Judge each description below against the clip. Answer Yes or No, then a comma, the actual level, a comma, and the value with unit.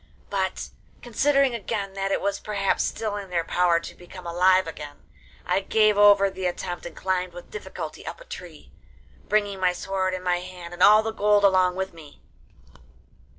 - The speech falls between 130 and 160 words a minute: No, average, 180 wpm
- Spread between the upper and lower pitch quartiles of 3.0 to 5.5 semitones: No, narrow, 2.4 semitones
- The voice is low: No, high, 190 Hz